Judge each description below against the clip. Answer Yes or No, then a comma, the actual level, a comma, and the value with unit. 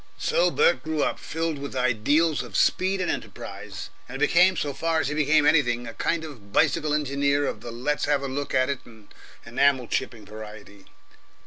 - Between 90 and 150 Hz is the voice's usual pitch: Yes, medium, 140 Hz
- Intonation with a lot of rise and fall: No, average, 4.6 semitones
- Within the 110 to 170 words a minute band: No, average, 190 wpm